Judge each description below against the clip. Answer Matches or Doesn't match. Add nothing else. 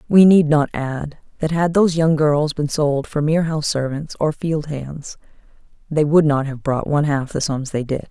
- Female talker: Matches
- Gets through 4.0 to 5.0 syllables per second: Matches